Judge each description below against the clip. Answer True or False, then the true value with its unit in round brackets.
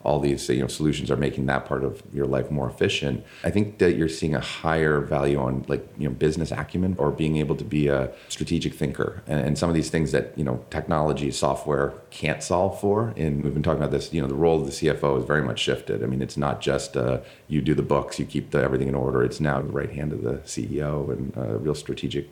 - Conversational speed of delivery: False (255 wpm)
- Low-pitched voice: True (75 Hz)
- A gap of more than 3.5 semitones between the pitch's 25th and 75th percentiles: False (2.4 semitones)